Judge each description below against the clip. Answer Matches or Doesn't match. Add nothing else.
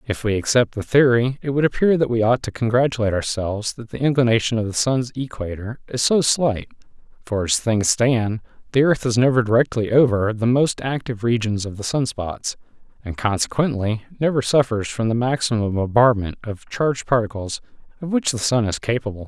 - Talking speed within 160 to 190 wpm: Matches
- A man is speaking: Matches